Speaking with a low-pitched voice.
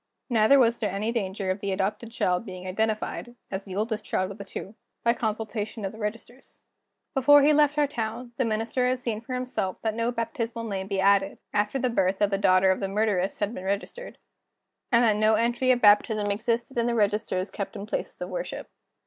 No: high, 215 Hz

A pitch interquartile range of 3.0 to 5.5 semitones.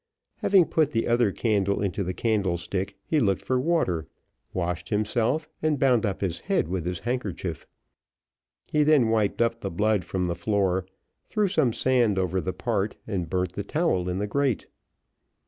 Yes: average, 5.2 semitones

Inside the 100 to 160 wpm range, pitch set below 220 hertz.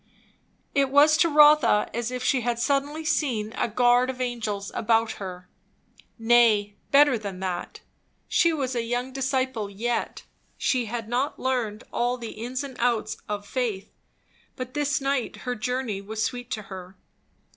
No: average, 155 wpm; high, 245 Hz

